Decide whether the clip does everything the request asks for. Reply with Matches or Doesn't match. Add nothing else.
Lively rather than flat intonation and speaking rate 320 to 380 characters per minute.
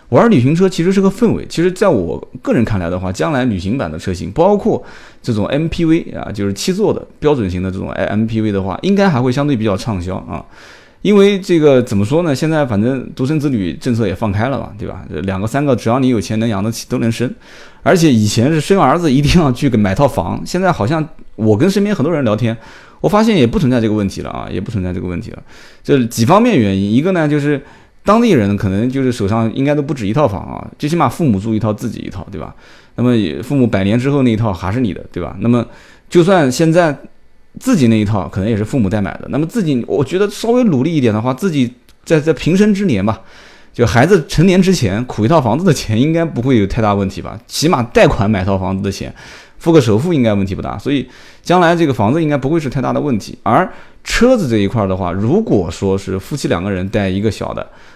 Matches